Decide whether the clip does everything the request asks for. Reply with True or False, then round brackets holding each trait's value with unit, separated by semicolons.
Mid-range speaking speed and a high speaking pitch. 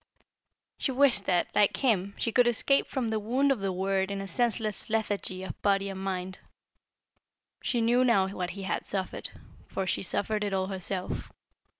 True (180 wpm; 200 Hz)